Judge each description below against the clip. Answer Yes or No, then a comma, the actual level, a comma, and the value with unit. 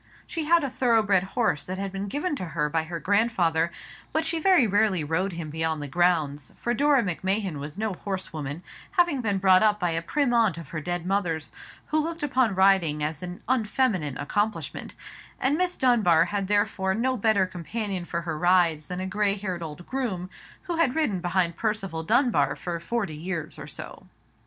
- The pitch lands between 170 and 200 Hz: Yes, high, 190 Hz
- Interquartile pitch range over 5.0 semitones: Yes, wide, 5.5 semitones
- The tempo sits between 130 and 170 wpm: No, average, 190 wpm